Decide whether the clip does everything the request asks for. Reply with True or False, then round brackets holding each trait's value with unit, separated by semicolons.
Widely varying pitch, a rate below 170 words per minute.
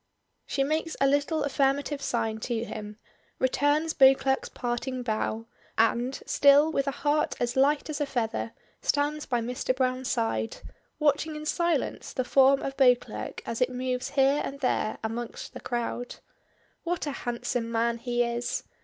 False (3.2 semitones; 155 wpm)